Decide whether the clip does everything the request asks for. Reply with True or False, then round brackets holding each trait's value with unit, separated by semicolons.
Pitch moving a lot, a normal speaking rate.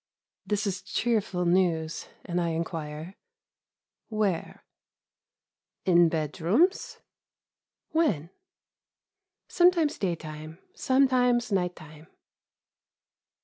False (6.4 semitones; 70 wpm)